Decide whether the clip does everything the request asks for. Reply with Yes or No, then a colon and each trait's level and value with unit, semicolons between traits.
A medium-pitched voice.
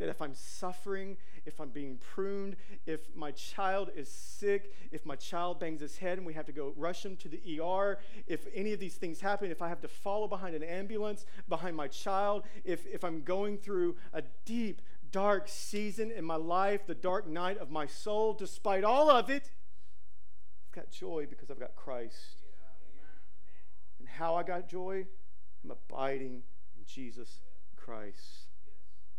Yes: medium, 170 Hz